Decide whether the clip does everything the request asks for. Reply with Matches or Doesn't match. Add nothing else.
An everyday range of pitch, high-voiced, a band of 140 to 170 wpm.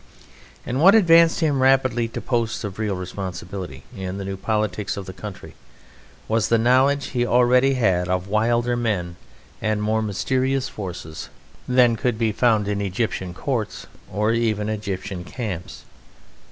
Doesn't match